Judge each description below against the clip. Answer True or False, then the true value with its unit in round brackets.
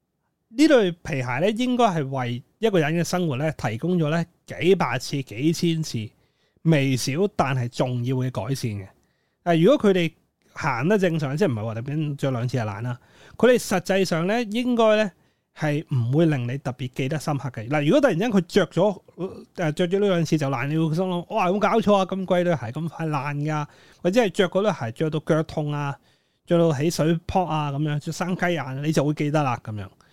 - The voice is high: False (160 Hz)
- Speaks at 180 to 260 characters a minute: False (295 characters per minute)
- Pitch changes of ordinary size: True (5.0 semitones)